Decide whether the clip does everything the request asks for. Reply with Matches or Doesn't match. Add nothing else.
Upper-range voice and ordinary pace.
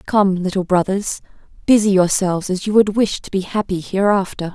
Matches